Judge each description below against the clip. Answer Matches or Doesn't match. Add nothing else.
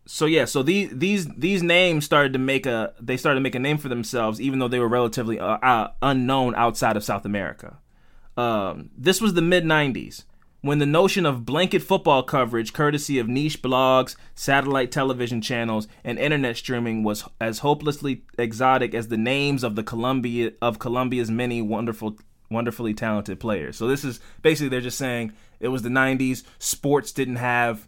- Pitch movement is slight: Doesn't match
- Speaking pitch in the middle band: Doesn't match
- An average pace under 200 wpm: Matches